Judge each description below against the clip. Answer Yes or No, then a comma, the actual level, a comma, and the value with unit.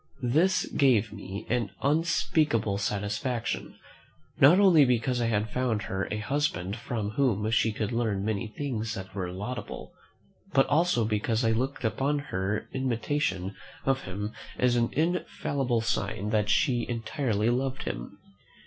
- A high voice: No, low, 115 Hz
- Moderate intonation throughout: Yes, average, 4.4 semitones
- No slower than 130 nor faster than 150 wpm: Yes, average, 140 wpm